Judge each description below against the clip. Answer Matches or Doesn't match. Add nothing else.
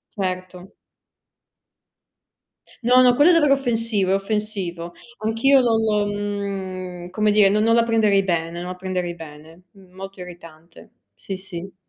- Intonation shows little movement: Doesn't match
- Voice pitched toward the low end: Doesn't match